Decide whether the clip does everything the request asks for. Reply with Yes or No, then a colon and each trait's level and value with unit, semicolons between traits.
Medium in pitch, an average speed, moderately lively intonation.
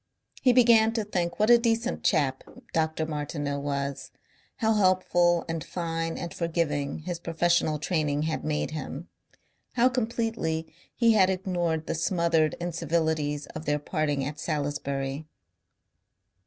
No: medium, 165 Hz; slow, 130 wpm; average, 3.7 semitones